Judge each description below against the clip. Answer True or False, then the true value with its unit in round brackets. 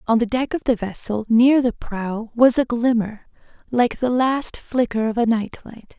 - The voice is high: True (235 Hz)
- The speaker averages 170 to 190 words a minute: False (200 wpm)